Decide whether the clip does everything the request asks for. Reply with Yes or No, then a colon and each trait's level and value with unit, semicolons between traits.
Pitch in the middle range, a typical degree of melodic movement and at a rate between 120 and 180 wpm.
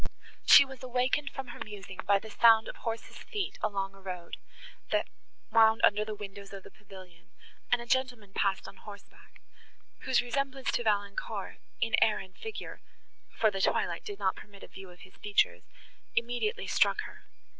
No: high, 210 Hz; average, 3.7 semitones; average, 175 wpm